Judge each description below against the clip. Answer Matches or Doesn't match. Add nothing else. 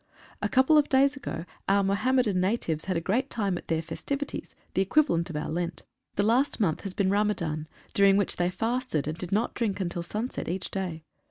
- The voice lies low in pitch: Doesn't match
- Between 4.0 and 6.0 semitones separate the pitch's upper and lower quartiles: Matches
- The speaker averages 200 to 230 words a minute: Matches